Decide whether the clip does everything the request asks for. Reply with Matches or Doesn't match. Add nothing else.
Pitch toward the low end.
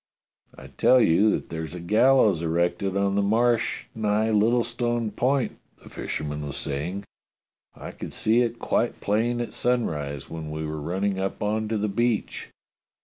Matches